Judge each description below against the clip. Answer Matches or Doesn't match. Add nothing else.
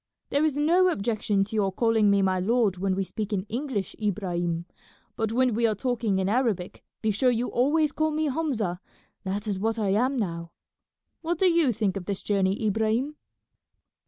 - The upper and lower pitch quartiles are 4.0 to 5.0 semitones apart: Matches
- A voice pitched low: Doesn't match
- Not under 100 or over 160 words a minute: Doesn't match